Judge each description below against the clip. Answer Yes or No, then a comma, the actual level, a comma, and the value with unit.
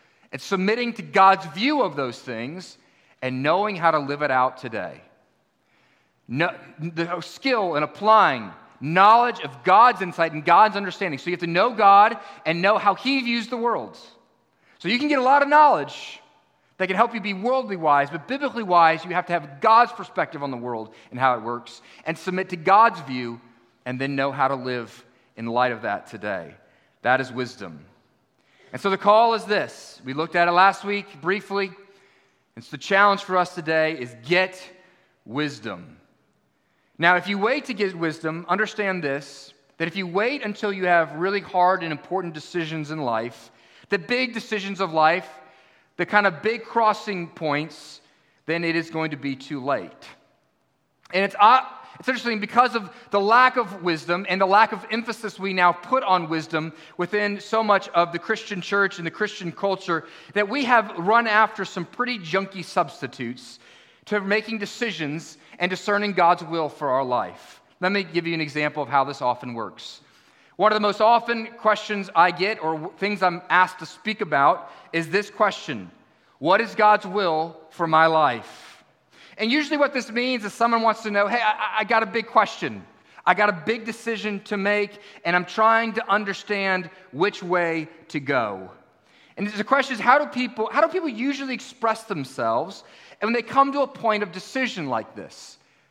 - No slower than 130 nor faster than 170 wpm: No, average, 185 wpm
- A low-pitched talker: No, high, 190 Hz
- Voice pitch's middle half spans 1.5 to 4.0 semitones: No, average, 5.3 semitones